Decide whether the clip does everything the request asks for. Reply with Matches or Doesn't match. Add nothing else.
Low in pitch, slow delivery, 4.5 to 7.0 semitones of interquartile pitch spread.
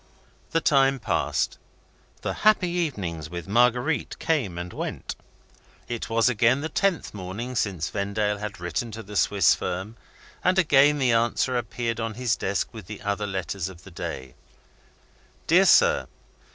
Doesn't match